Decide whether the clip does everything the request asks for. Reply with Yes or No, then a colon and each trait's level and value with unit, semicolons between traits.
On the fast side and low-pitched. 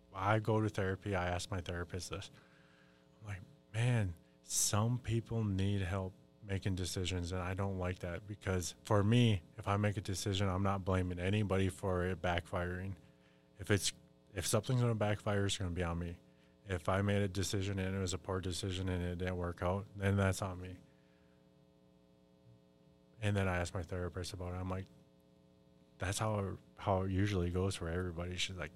No: average, 190 wpm; very low, 95 Hz